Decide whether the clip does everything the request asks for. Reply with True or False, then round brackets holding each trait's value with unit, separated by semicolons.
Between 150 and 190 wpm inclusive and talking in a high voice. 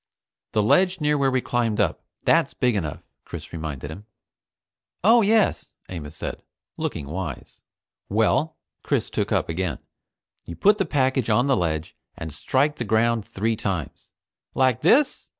False (155 wpm; 115 Hz)